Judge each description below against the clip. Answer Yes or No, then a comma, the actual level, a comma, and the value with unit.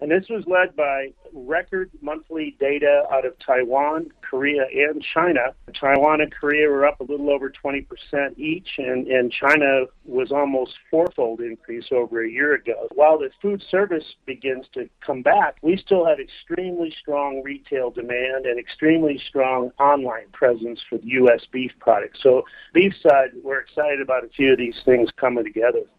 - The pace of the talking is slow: No, average, 170 wpm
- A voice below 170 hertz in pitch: Yes, medium, 140 Hz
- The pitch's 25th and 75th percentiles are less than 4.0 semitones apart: Yes, average, 3.5 semitones